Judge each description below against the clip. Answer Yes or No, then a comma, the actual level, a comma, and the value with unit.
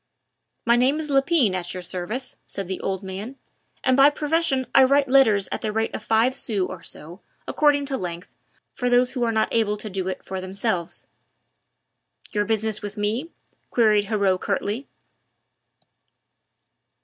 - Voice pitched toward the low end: No, high, 220 Hz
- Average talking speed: Yes, average, 160 wpm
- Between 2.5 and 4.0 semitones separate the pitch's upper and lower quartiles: No, average, 5.1 semitones